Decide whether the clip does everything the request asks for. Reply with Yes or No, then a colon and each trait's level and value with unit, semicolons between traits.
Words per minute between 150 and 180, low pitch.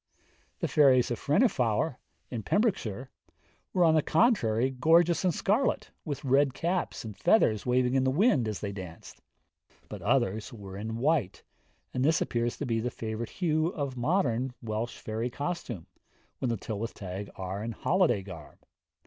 Yes: average, 160 wpm; low, 125 Hz